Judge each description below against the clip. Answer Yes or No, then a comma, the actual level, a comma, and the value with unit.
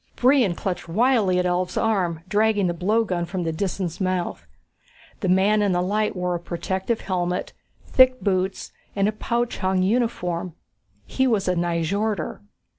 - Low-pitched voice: No, high, 190 Hz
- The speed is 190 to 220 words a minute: No, average, 155 wpm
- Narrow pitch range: No, average, 3.2 semitones